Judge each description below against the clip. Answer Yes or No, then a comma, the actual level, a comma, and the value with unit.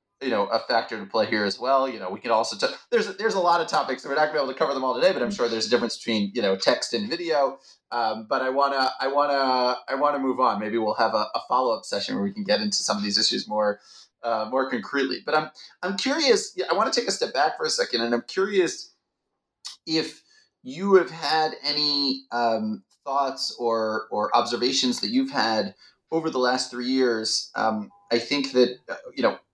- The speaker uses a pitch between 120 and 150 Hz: Yes, low, 135 Hz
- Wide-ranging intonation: Yes, wide, 8.0 semitones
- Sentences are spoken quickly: Yes, fast, 240 wpm